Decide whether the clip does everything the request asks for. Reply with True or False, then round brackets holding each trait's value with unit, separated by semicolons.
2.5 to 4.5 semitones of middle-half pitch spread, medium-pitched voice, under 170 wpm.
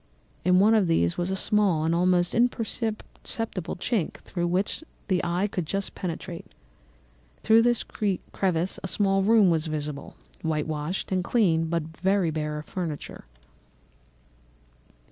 True (3.7 semitones; 180 Hz; 135 wpm)